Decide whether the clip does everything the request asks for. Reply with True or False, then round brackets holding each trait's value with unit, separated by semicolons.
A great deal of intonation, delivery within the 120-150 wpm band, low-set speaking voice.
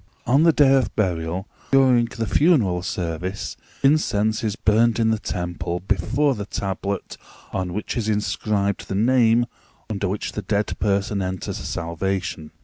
False (4.0 semitones; 145 wpm; 105 Hz)